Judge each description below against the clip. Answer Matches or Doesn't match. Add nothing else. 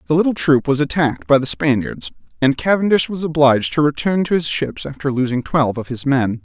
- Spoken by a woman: Doesn't match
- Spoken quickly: Matches